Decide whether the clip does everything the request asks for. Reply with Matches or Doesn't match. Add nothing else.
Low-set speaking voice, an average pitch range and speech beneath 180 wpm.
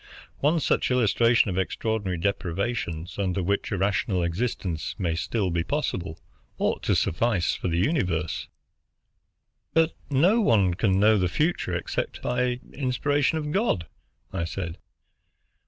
Doesn't match